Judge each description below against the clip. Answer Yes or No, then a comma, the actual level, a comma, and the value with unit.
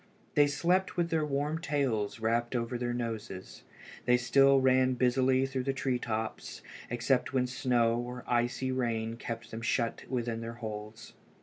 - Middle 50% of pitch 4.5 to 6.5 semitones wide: No, narrow, 2.4 semitones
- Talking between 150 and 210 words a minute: Yes, average, 160 wpm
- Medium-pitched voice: No, low, 125 Hz